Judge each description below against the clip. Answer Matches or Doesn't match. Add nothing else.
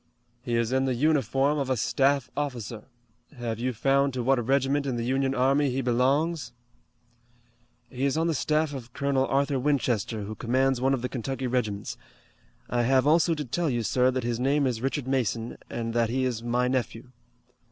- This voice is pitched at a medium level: Doesn't match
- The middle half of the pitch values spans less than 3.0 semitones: Matches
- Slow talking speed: Doesn't match